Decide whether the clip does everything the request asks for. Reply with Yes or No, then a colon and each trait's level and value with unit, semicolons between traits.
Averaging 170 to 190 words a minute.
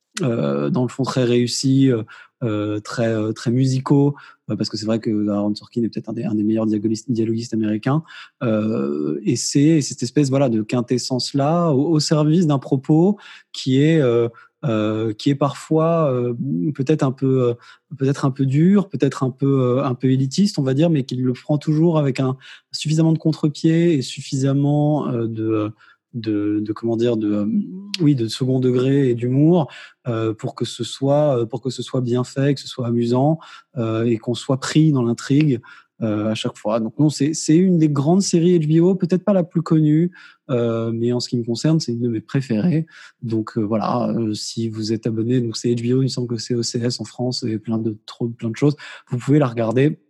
No: average, 210 wpm